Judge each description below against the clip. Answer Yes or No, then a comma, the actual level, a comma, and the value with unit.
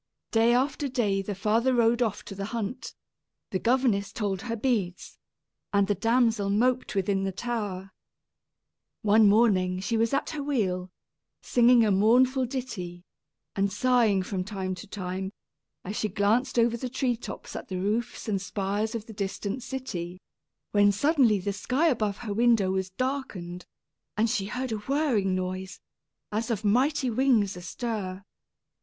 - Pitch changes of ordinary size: Yes, average, 3.9 semitones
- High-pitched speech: Yes, high, 215 Hz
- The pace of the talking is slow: No, average, 155 wpm